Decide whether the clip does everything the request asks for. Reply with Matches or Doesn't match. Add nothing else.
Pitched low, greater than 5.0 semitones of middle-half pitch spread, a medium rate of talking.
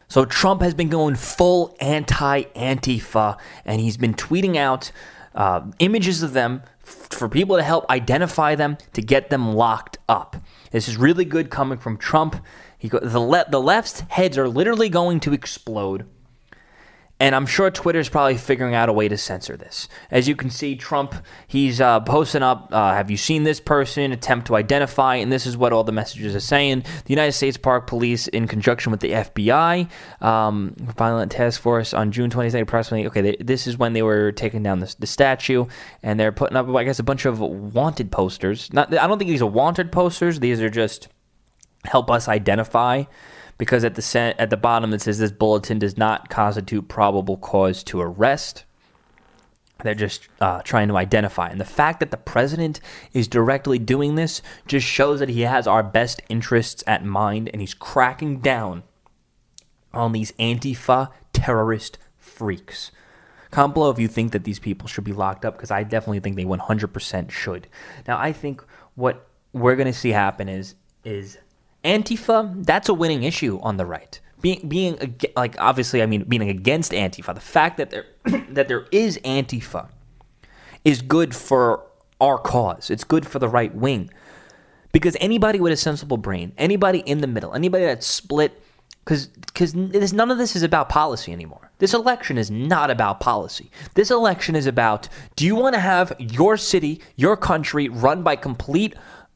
Matches